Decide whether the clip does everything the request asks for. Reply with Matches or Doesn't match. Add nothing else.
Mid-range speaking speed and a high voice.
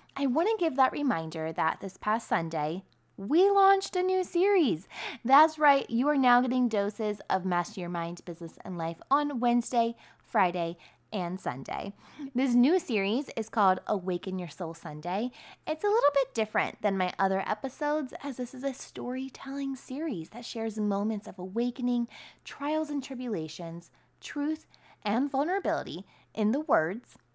Matches